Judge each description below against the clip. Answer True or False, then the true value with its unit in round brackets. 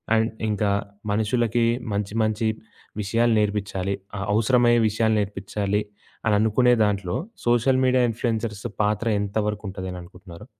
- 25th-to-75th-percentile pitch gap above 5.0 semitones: False (2.4 semitones)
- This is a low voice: True (105 Hz)